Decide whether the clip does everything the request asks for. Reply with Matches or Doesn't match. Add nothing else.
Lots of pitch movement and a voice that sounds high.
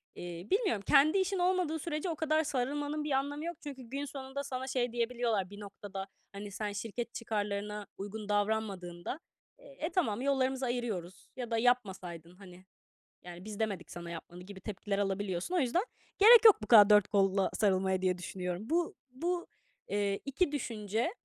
Matches